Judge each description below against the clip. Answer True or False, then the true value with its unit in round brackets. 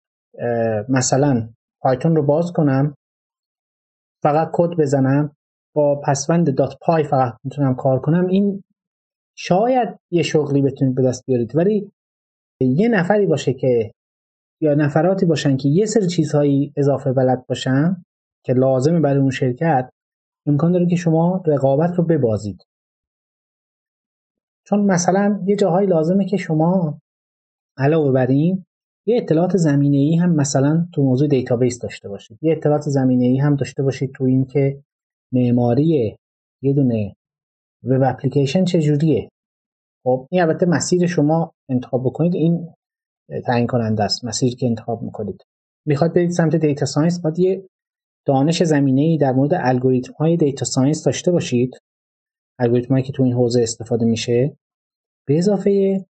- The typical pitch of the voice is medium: True (145 Hz)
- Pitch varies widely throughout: False (4.9 semitones)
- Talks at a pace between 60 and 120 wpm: False (140 wpm)